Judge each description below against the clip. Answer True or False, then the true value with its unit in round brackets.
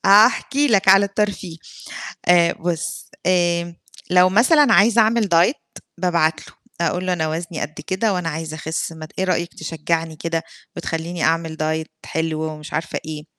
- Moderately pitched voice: True (170 Hz)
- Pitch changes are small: False (3.0 semitones)